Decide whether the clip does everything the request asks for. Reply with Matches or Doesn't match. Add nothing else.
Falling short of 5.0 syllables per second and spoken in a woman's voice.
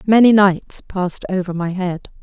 Matches